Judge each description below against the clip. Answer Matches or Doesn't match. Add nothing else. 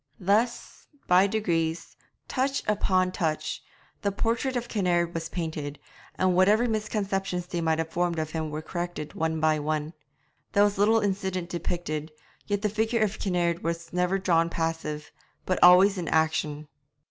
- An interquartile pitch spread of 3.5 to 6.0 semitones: Matches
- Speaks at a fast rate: Doesn't match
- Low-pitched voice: Doesn't match